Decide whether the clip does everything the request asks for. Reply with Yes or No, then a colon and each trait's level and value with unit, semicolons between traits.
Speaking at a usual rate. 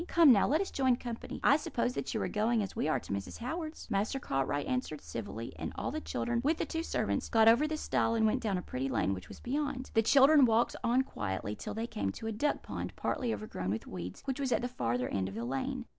No: fast, 255 wpm